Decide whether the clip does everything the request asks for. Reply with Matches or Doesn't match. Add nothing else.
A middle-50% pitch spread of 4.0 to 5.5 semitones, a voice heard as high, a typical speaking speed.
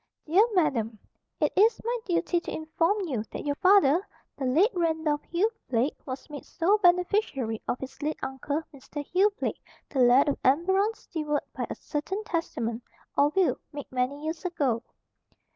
Matches